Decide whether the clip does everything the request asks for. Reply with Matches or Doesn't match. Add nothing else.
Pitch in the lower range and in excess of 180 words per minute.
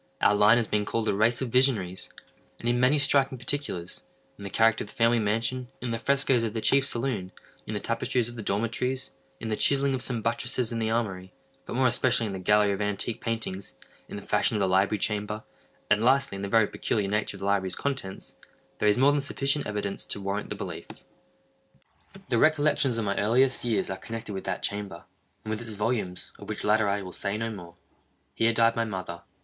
Matches